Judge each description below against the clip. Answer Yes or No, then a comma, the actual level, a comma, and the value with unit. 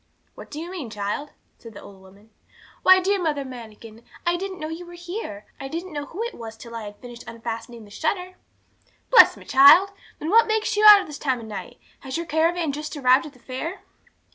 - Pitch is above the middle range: Yes, very high, 295 Hz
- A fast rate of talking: Yes, fast, 220 wpm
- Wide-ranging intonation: Yes, wide, 7.4 semitones